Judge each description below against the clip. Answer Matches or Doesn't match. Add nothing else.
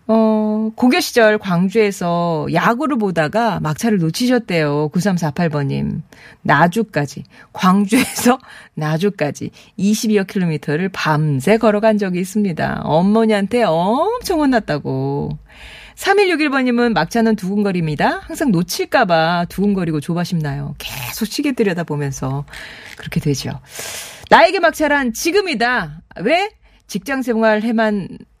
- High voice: Matches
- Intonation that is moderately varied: Doesn't match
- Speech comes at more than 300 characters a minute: Doesn't match